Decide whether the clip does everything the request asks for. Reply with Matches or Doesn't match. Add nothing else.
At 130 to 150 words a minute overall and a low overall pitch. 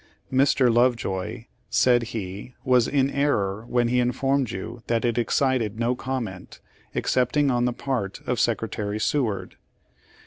Matches